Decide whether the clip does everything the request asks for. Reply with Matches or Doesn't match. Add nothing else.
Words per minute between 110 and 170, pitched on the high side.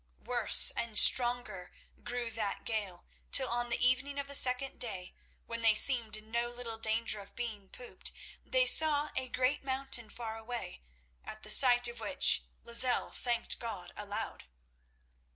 Matches